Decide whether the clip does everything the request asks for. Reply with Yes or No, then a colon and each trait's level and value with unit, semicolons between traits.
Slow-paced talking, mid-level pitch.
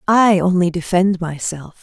Yes: slow, 130 wpm; medium, 180 Hz